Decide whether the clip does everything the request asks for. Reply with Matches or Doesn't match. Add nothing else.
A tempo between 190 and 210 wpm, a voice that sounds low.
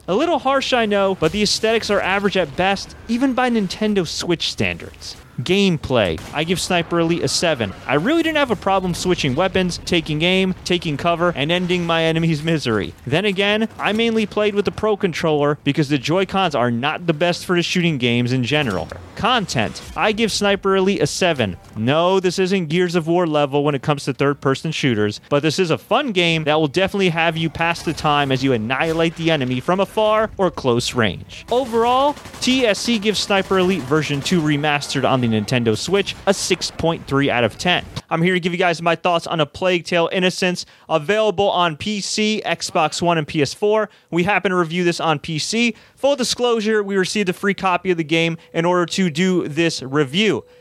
Doesn't match